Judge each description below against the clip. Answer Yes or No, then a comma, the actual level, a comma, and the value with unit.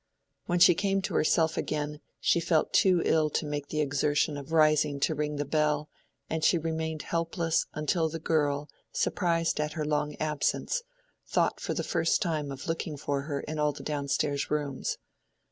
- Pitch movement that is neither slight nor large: No, narrow, 1.9 semitones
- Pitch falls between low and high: Yes, medium, 155 Hz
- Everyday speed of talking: Yes, average, 180 wpm